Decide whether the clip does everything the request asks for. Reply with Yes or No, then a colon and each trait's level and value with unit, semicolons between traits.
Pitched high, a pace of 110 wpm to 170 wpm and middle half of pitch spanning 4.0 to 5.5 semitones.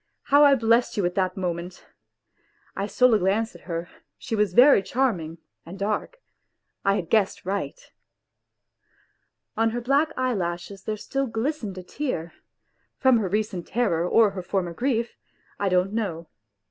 Yes: high, 205 Hz; average, 155 wpm; average, 4.9 semitones